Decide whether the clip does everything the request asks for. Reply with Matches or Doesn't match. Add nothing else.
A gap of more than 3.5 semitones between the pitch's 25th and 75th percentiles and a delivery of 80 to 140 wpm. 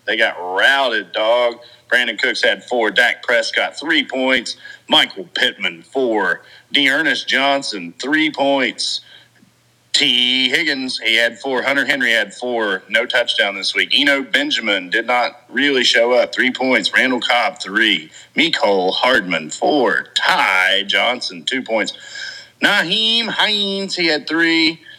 Matches